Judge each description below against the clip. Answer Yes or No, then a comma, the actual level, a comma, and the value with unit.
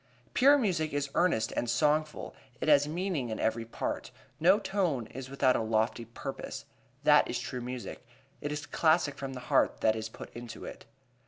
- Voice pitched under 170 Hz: Yes, medium, 140 Hz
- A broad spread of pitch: No, average, 4.9 semitones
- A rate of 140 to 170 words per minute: No, average, 180 wpm